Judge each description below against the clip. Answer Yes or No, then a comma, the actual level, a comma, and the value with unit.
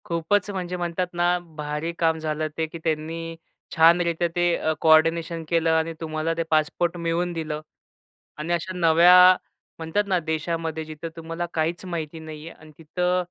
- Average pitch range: No, narrow, 1.6 semitones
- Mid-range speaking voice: Yes, medium, 165 Hz